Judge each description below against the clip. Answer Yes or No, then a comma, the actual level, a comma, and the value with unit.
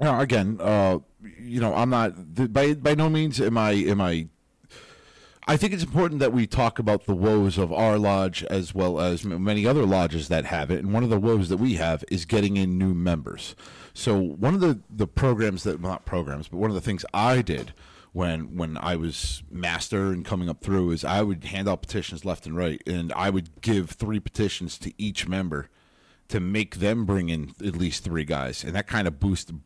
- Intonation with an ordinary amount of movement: Yes, average, 4.1 semitones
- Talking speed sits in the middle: No, fast, 220 wpm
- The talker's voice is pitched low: Yes, very low, 95 Hz